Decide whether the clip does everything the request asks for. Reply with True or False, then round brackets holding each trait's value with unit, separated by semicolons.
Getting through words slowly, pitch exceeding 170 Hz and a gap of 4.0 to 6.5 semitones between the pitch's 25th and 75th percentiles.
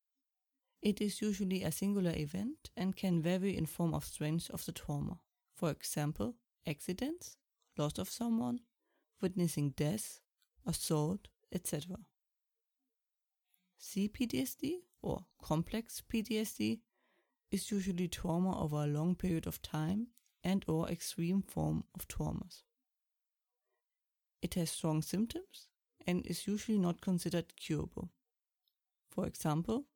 True (110 wpm; 185 Hz; 5.5 semitones)